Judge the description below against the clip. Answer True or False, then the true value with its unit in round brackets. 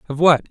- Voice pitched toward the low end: False (150 Hz)